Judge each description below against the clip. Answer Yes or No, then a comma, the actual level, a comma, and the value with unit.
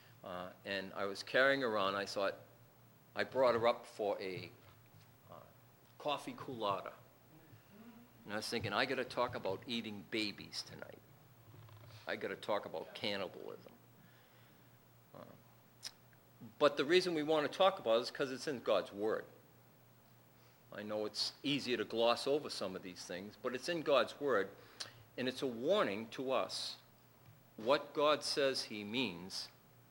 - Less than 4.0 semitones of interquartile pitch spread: No, average, 4.5 semitones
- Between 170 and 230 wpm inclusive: No, average, 150 wpm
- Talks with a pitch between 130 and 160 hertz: No, low, 120 Hz